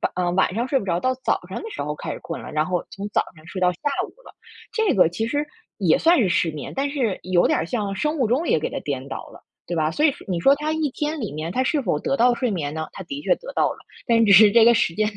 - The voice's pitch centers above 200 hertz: Yes, high, 215 Hz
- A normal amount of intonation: No, wide, 8.1 semitones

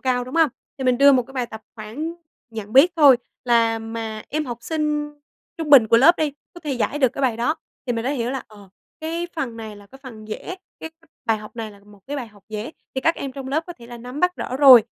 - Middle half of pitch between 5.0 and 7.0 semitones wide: No, average, 4.5 semitones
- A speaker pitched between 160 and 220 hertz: No, very high, 255 Hz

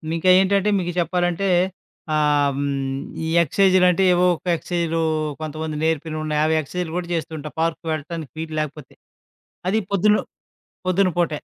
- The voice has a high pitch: No, medium, 165 Hz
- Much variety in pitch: No, average, 2.8 semitones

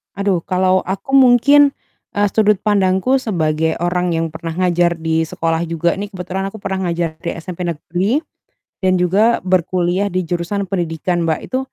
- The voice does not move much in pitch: No, average, 3.0 semitones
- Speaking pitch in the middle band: Yes, medium, 180 Hz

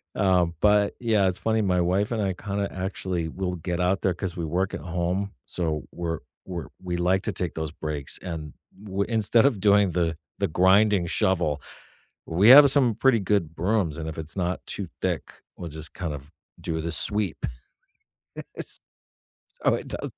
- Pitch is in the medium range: No, very low, 90 Hz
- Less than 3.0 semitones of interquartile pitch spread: No, average, 3.3 semitones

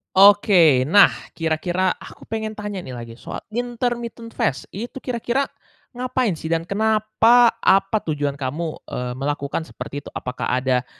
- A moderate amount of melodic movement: No, wide, 7.4 semitones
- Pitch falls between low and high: No, high, 195 Hz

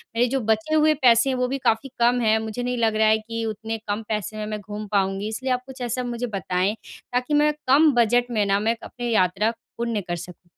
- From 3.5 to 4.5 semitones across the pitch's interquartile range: No, average, 2.7 semitones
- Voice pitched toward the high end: Yes, high, 225 Hz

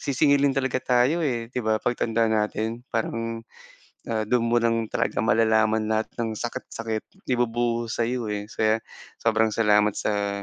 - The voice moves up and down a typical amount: No, narrow, 1.6 semitones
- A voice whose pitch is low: Yes, low, 115 Hz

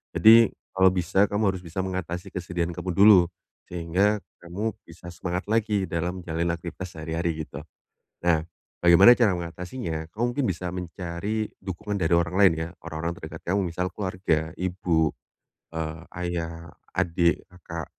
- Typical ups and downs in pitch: No, narrow, 2.2 semitones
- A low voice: Yes, very low, 90 Hz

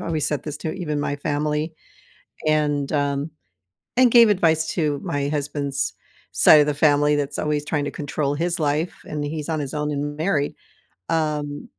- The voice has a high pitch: No, medium, 150 Hz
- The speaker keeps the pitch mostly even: Yes, narrow, 1.5 semitones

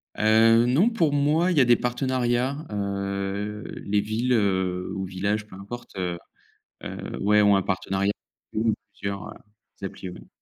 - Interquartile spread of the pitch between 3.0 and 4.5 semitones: Yes, average, 3.8 semitones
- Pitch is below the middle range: Yes, low, 105 Hz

